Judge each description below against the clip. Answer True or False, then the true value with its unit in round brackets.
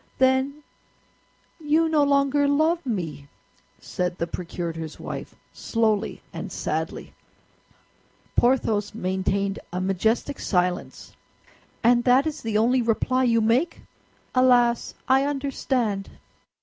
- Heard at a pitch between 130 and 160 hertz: False (240 Hz)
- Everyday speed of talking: False (105 wpm)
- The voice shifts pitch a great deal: True (5.9 semitones)